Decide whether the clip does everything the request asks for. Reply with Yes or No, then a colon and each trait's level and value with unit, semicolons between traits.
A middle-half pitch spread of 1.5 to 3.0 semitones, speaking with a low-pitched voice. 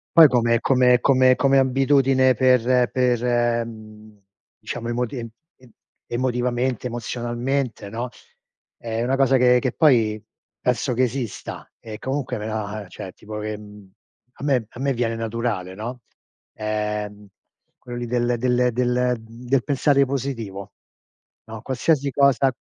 Yes: narrow, 2.5 semitones; low, 120 Hz